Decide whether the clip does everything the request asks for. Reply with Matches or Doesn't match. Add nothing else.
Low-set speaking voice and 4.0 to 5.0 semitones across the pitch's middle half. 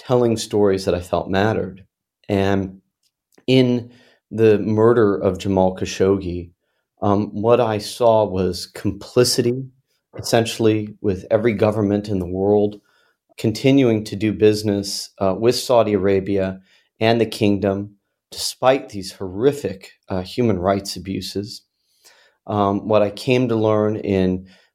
Doesn't match